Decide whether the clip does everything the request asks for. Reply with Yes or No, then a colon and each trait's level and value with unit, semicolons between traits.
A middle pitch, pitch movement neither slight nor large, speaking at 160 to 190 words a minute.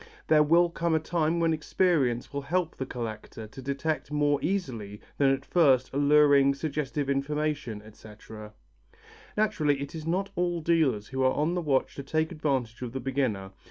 Yes: medium, 145 Hz; average, 3.6 semitones; average, 170 wpm